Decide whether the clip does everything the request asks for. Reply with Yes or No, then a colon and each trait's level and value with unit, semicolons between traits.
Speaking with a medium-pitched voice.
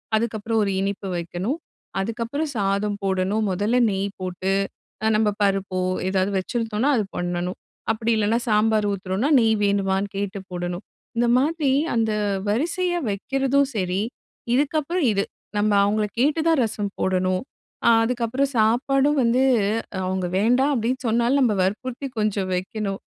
No: high, 215 Hz